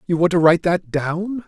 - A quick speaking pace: Yes, fast, 245 wpm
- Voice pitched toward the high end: No, medium, 175 Hz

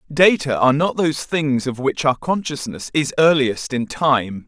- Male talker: Yes, male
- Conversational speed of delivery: Yes, average, 175 wpm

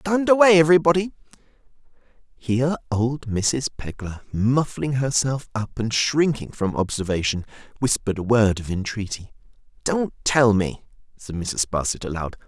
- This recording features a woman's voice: No, male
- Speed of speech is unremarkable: No, slow, 125 wpm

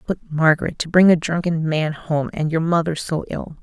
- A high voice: No, medium, 165 Hz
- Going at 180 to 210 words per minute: Yes, average, 200 wpm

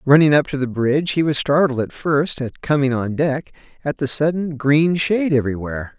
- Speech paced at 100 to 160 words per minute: No, average, 200 wpm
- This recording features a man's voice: Yes, male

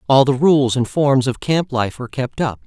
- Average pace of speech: No, fast, 250 wpm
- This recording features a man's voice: Yes, male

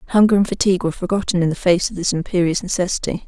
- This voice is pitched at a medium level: Yes, medium, 180 Hz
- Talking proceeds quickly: Yes, fast, 220 wpm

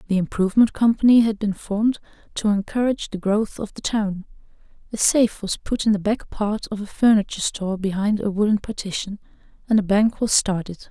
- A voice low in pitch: No, high, 210 Hz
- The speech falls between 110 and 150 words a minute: No, average, 185 wpm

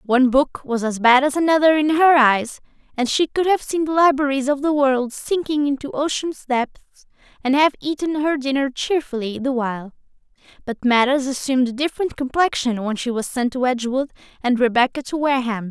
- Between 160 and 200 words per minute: Yes, average, 185 wpm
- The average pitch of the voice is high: Yes, very high, 270 Hz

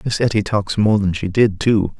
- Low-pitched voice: Yes, low, 105 Hz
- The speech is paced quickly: Yes, fast, 240 wpm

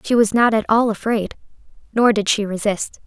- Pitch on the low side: No, high, 215 Hz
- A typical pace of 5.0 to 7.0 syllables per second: Yes, 5.1 syllables/s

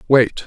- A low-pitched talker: Yes, low, 130 Hz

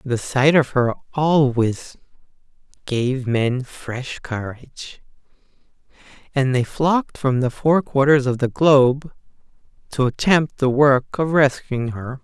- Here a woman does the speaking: No, male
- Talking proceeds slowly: Yes, slow, 130 wpm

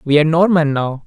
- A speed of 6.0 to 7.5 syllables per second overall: Yes, 6.2 syllables/s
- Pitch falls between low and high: Yes, medium, 155 Hz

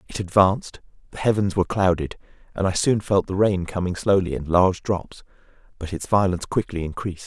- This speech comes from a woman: No, male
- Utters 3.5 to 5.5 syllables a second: No, 5.9 syllables/s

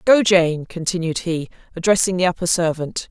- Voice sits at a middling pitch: Yes, medium, 175 Hz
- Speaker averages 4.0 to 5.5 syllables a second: Yes, 5.1 syllables/s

